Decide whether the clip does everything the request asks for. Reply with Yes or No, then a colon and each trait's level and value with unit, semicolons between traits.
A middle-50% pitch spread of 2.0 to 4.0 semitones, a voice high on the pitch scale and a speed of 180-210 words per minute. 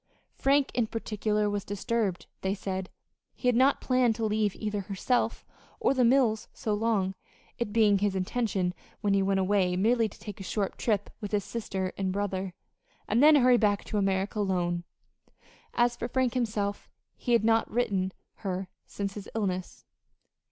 No: average, 3.2 semitones; high, 205 Hz; average, 170 wpm